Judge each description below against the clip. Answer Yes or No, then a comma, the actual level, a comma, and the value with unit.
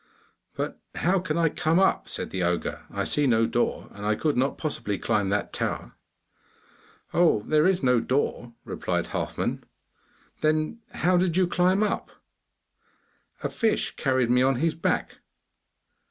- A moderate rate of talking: Yes, average, 155 wpm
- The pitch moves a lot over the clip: Yes, wide, 6.8 semitones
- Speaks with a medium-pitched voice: Yes, medium, 150 Hz